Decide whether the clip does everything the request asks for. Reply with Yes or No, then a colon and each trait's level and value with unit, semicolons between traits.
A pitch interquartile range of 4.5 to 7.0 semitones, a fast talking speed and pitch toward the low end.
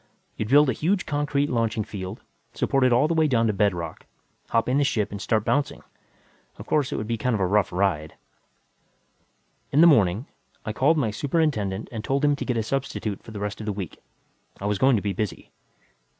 Yes: wide, 5.5 semitones; fast, 210 wpm; low, 115 Hz